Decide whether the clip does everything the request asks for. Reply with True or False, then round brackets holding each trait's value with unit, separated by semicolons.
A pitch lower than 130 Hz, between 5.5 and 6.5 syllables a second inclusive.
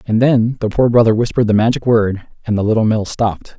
True (110 Hz; 6.2 syllables/s)